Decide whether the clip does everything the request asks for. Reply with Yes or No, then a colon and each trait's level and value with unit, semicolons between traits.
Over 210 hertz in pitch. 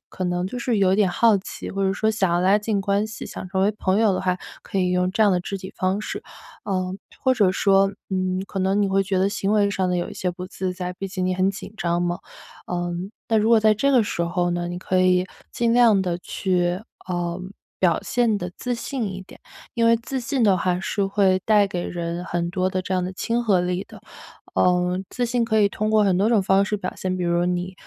No: high, 190 Hz